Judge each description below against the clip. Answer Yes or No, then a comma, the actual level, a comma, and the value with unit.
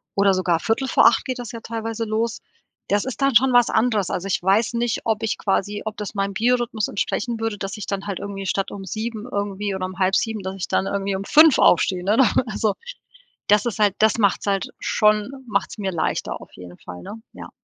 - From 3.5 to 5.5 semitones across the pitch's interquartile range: No, narrow, 2.6 semitones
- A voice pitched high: Yes, high, 210 Hz